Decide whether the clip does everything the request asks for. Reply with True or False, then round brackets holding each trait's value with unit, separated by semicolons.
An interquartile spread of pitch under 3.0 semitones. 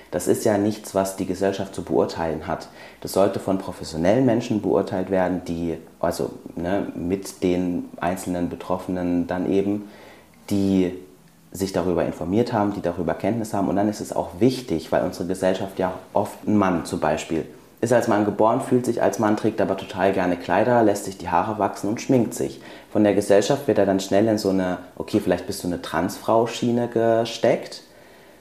True (2.6 semitones)